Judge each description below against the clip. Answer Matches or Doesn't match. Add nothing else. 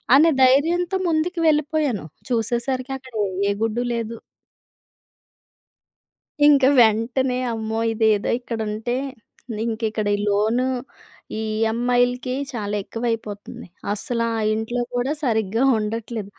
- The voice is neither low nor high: Doesn't match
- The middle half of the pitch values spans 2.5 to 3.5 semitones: Matches